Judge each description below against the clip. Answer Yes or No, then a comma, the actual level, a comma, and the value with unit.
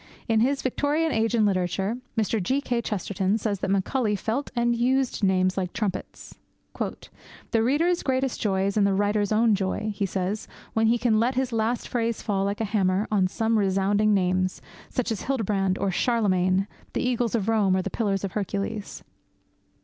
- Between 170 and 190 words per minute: Yes, average, 180 wpm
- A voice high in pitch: Yes, high, 215 Hz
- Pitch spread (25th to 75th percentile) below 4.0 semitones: Yes, average, 3.3 semitones